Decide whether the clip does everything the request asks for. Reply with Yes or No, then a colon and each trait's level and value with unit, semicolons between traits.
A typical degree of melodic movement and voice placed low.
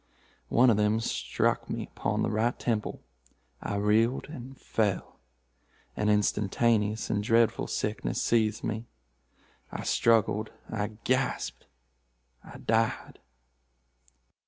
No: narrow, 1.9 semitones; low, 110 Hz